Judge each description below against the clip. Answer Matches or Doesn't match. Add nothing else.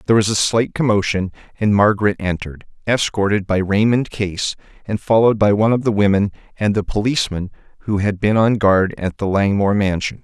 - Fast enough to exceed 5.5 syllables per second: Matches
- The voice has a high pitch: Doesn't match